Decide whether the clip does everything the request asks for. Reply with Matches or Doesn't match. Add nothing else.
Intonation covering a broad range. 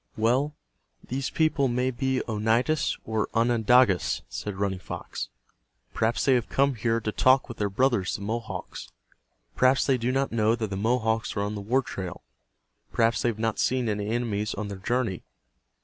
Doesn't match